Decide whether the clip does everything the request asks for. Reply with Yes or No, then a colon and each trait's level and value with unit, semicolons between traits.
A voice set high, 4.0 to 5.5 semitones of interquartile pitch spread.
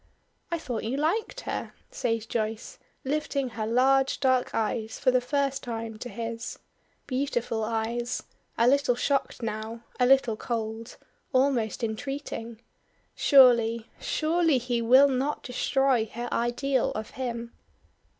No: high, 245 Hz; average, 3.0 semitones